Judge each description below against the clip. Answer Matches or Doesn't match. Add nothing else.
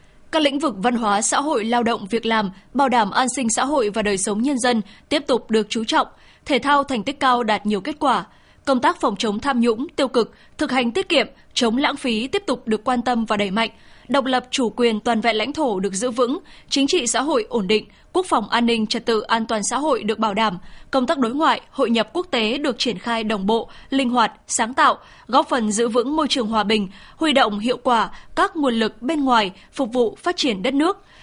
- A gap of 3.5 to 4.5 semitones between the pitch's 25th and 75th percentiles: Matches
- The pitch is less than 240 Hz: Doesn't match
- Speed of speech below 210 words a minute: Doesn't match